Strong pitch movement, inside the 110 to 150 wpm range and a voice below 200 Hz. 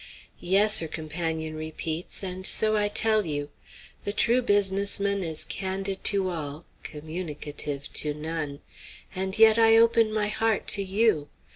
No: average, 4.9 semitones; average, 145 wpm; high, 190 Hz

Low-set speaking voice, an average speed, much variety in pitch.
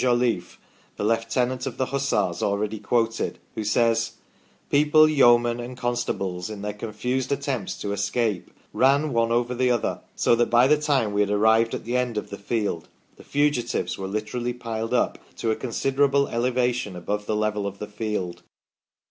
No: low, 115 Hz; average, 175 wpm; average, 3.0 semitones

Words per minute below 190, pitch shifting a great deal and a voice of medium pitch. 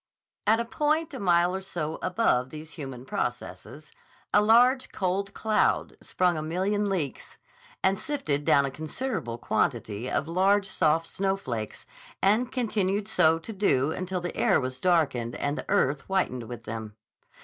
Yes: average, 155 wpm; wide, 6.4 semitones; medium, 175 Hz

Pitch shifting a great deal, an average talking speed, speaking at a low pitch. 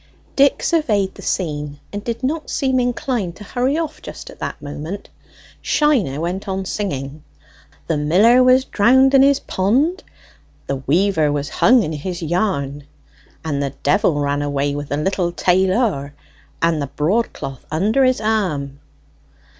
No: wide, 8.8 semitones; average, 155 wpm; medium, 185 Hz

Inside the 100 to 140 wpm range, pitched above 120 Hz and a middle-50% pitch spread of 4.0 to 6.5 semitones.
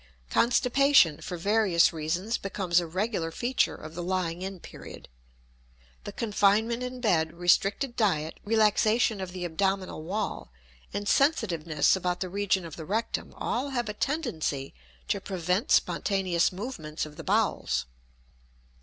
Yes: slow, 135 wpm; high, 190 Hz; average, 4.7 semitones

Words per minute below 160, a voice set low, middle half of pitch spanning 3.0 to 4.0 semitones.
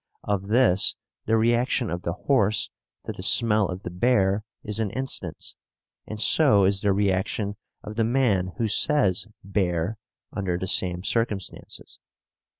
Yes: average, 150 wpm; low, 100 Hz; average, 3.3 semitones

